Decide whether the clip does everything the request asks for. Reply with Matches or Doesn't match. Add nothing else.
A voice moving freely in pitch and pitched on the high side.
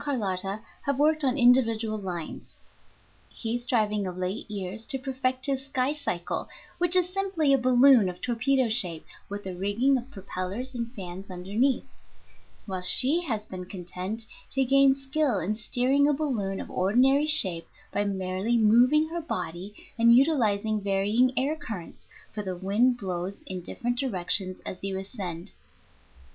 Matches